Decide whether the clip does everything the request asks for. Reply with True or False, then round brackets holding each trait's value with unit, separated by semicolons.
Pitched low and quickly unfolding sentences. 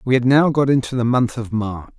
True (120 Hz; 270 wpm)